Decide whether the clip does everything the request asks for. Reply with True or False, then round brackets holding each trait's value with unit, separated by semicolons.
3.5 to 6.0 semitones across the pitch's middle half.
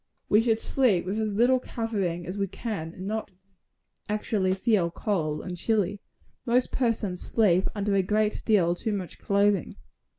False (3.1 semitones)